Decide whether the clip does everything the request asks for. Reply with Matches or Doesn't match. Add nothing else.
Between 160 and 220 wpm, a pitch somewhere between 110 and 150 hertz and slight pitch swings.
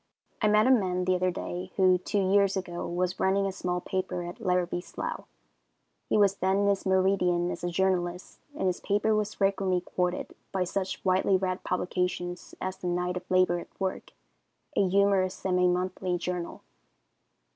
Doesn't match